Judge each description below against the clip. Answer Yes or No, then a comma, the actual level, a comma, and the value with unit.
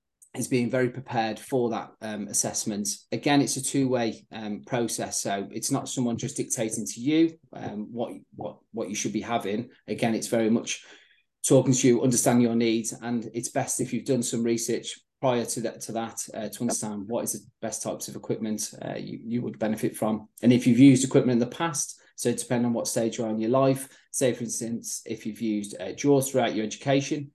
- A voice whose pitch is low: Yes, low, 120 Hz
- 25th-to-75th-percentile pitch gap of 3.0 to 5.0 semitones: No, narrow, 2.6 semitones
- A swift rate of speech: Yes, fast, 215 wpm